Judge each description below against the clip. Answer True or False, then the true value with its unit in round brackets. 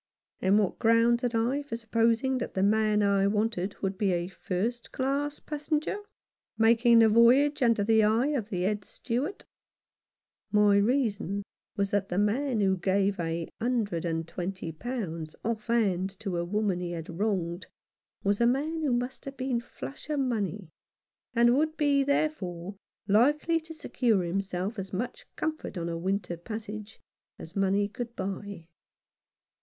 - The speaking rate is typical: True (160 wpm)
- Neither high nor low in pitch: False (215 Hz)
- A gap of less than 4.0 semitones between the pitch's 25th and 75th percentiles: False (4.4 semitones)